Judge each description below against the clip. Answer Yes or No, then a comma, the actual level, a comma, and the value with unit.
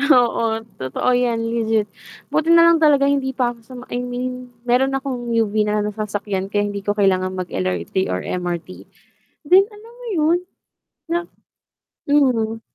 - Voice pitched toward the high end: Yes, high, 240 Hz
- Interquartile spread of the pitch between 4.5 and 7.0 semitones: Yes, average, 5.2 semitones